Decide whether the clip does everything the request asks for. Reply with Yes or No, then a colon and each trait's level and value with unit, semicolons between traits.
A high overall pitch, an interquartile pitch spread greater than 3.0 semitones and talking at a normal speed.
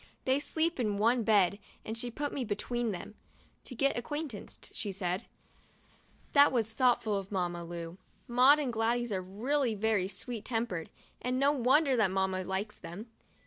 Yes: high, 225 Hz; average, 4.6 semitones; average, 165 wpm